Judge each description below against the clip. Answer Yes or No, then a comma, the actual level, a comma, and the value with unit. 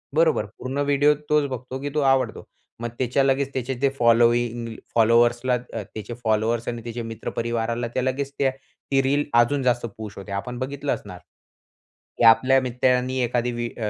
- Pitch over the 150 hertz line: No, low, 120 Hz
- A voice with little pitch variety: Yes, narrow, 2.2 semitones